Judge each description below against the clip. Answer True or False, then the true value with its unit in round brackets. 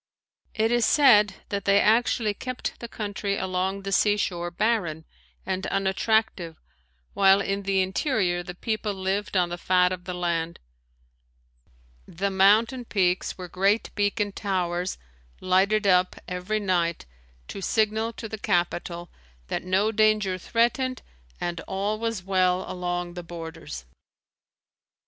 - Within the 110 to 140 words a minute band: True (135 wpm)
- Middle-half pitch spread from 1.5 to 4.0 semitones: True (3.0 semitones)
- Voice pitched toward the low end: False (195 Hz)